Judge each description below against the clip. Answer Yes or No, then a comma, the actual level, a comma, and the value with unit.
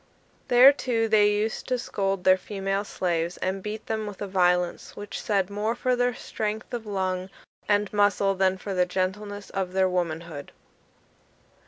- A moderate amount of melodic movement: No, narrow, 2.3 semitones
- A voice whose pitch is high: Yes, high, 200 Hz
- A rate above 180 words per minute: No, average, 165 wpm